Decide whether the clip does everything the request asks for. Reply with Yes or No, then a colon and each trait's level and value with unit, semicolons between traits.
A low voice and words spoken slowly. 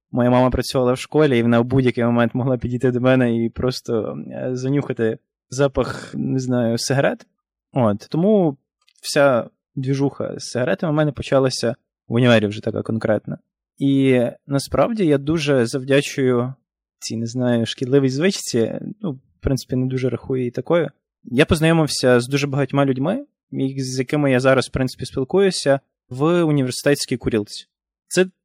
No: low, 130 Hz; average, 150 wpm